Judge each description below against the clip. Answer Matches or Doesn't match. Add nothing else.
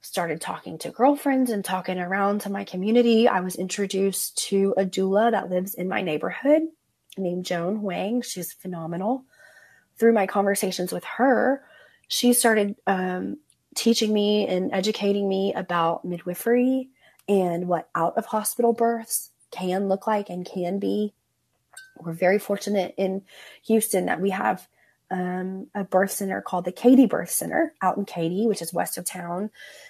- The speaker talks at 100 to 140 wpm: Doesn't match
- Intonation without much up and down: Doesn't match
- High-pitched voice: Matches